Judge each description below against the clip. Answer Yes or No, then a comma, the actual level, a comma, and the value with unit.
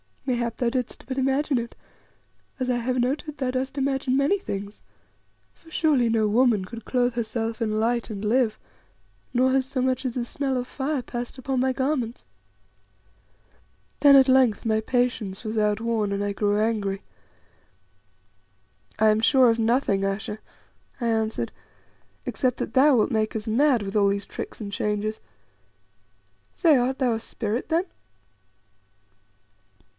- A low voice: No, high, 240 Hz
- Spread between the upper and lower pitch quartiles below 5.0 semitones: Yes, average, 3.3 semitones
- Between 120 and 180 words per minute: Yes, average, 155 wpm